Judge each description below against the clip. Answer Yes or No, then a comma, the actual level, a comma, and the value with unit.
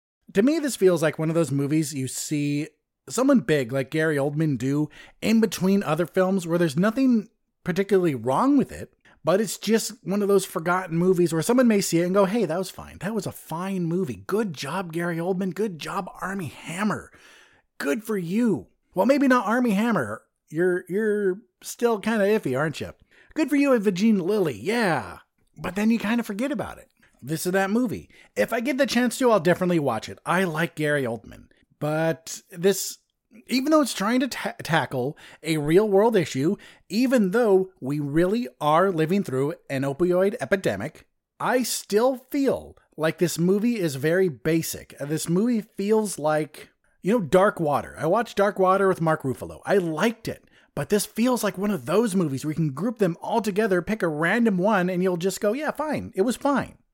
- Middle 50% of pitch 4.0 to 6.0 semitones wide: Yes, wide, 5.6 semitones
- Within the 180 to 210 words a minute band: Yes, average, 195 wpm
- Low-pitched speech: No, high, 190 Hz